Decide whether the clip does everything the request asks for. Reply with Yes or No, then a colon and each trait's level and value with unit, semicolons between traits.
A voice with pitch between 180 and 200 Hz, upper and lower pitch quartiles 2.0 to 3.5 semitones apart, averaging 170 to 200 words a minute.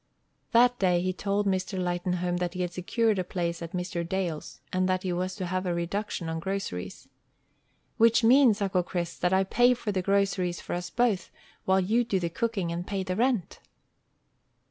Yes: medium, 185 Hz; narrow, 2.4 semitones; average, 190 wpm